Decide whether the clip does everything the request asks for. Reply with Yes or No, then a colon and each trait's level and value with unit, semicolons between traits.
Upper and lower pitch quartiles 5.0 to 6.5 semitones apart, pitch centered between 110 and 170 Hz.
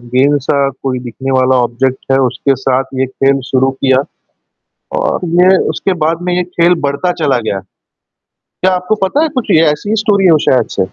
Yes: wide, 5.4 semitones; medium, 140 Hz